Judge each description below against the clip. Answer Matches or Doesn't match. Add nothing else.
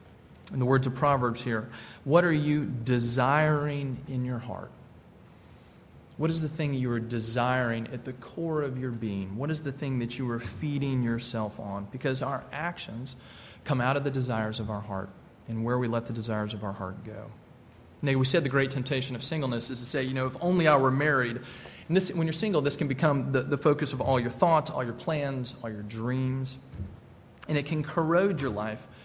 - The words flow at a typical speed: Doesn't match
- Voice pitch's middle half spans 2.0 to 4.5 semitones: Matches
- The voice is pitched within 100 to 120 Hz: Doesn't match